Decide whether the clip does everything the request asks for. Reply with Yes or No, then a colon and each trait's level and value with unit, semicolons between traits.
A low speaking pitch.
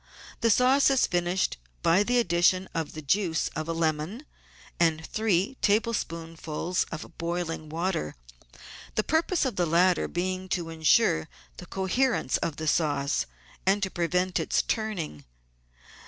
No: medium, 175 Hz